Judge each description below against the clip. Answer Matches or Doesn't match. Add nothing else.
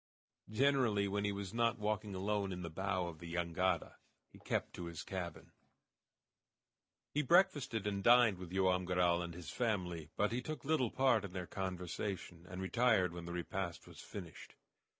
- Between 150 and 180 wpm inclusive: Matches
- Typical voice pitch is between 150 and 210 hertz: Doesn't match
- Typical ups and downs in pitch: Matches